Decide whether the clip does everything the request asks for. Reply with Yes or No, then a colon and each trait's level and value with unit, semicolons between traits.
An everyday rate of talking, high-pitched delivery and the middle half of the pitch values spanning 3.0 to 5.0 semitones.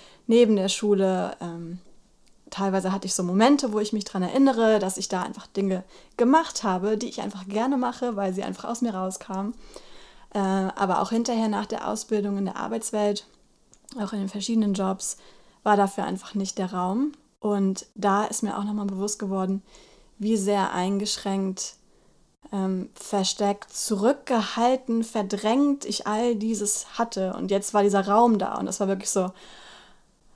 No: average, 165 wpm; high, 205 Hz; narrow, 2.6 semitones